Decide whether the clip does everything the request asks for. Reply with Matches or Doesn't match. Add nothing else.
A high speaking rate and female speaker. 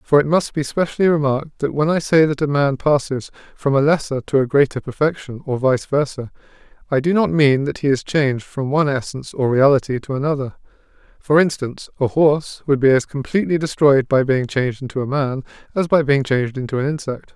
Doesn't match